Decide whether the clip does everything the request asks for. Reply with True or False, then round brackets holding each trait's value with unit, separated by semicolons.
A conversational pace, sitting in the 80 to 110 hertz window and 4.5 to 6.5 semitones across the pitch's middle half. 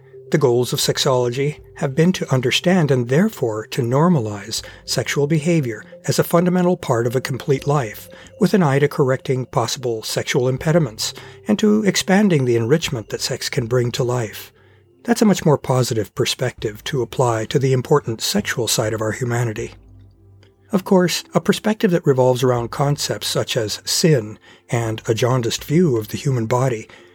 False (170 wpm; 130 Hz; 5.4 semitones)